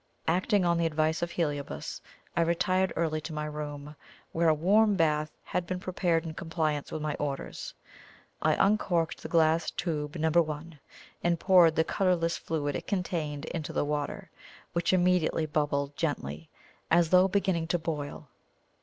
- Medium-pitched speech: Yes, medium, 165 Hz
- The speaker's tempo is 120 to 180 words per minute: Yes, average, 160 wpm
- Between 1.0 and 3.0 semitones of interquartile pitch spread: Yes, narrow, 2.6 semitones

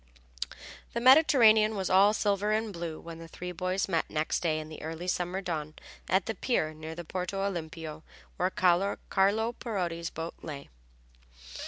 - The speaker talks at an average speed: Yes, average, 160 wpm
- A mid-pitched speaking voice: Yes, medium, 180 Hz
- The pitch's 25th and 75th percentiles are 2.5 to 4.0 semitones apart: Yes, average, 3.7 semitones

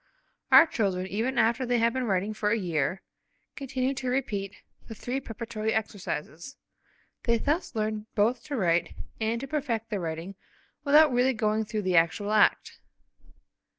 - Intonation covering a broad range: No, average, 3.9 semitones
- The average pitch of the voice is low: No, high, 220 Hz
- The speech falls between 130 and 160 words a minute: Yes, average, 155 wpm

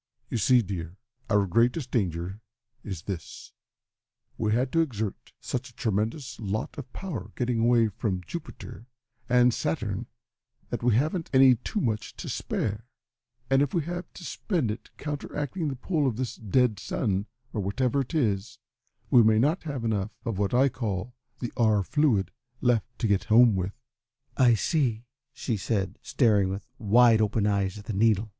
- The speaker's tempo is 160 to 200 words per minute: Yes, average, 170 wpm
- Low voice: Yes, low, 115 Hz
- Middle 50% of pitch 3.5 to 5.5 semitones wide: Yes, average, 4.1 semitones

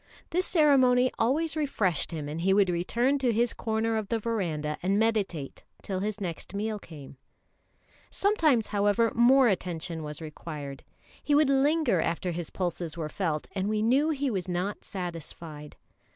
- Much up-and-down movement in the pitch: Yes, wide, 6.6 semitones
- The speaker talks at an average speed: Yes, average, 160 wpm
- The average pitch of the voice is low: No, high, 205 Hz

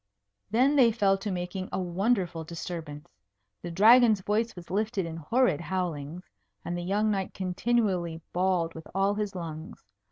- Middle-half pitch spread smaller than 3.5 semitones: No, average, 3.9 semitones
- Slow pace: No, average, 155 wpm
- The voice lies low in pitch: No, medium, 185 Hz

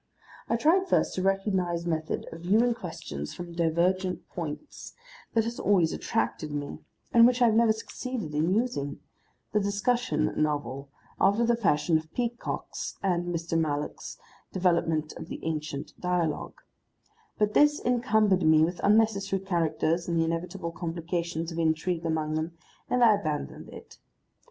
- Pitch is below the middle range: No, medium, 175 Hz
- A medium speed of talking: Yes, average, 145 wpm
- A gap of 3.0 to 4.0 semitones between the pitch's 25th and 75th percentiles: No, average, 5.1 semitones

